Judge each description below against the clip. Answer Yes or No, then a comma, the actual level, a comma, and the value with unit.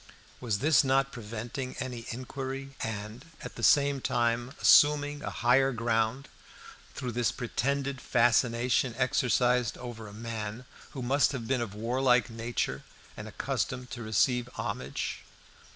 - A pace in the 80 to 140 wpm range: Yes, slow, 135 wpm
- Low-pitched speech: Yes, low, 125 Hz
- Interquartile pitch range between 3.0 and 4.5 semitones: No, narrow, 2.5 semitones